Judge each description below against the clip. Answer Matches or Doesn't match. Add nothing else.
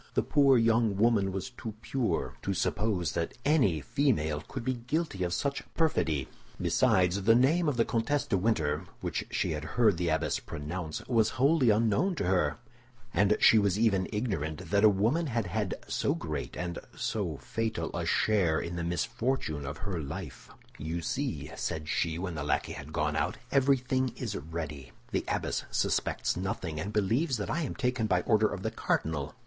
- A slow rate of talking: Doesn't match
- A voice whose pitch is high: Doesn't match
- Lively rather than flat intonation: Matches